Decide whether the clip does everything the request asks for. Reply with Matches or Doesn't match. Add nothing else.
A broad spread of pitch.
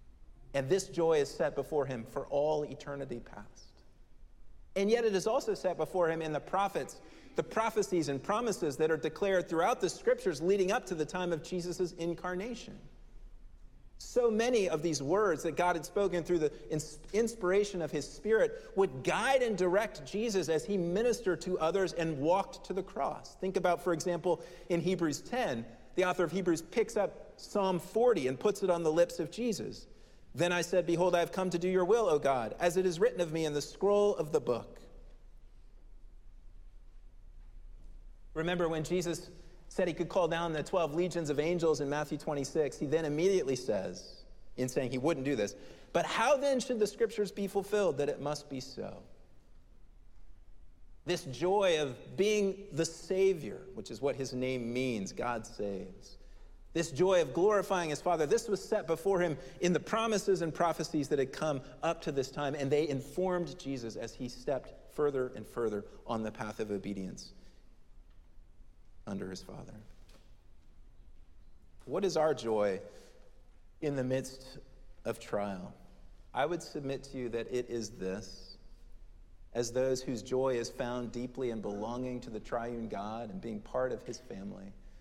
Matches